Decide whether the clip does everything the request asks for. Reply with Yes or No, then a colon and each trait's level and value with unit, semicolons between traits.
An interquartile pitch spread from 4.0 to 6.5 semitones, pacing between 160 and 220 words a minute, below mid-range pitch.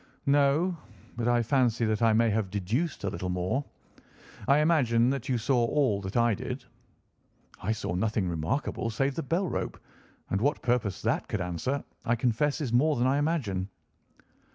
Yes: average, 4.8 semitones; average, 175 wpm; low, 120 Hz